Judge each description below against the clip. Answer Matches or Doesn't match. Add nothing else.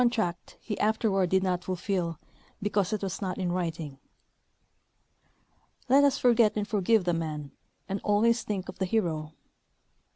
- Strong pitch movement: Doesn't match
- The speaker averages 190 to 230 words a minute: Doesn't match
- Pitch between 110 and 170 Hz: Doesn't match